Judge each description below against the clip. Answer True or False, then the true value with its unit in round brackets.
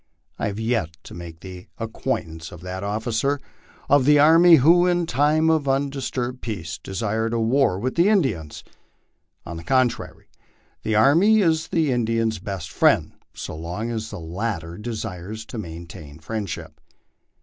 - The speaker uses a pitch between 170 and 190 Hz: False (110 Hz)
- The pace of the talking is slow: False (155 wpm)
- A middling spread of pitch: False (7.4 semitones)